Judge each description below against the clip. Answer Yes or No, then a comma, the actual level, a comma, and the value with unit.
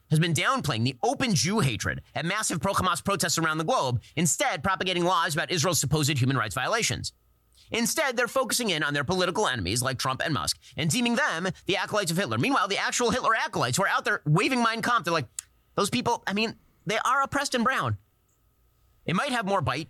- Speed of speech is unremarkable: No, fast, 215 wpm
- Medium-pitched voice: Yes, medium, 175 Hz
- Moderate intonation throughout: No, wide, 8.2 semitones